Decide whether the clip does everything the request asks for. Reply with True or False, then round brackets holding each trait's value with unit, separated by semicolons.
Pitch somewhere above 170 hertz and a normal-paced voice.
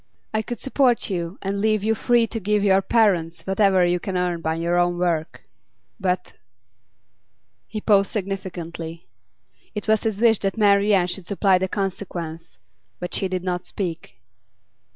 True (190 Hz; 160 wpm)